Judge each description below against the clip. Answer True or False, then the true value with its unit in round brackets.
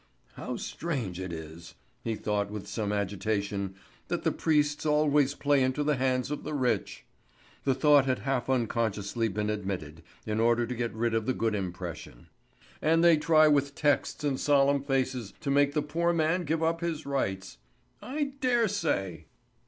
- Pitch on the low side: True (130 Hz)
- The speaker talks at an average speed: True (170 wpm)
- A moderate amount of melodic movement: False (6.2 semitones)